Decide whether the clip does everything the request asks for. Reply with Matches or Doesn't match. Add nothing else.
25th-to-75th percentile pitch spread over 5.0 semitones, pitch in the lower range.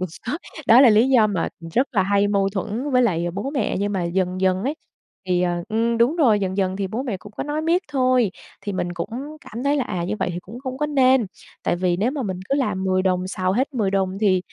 Doesn't match